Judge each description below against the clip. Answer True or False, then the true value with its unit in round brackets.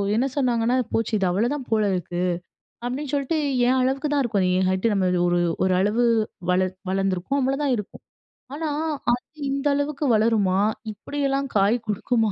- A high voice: True (230 Hz)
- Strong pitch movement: True (5.8 semitones)